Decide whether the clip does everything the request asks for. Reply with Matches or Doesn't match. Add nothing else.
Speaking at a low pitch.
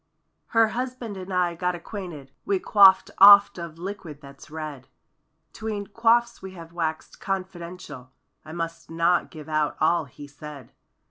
Doesn't match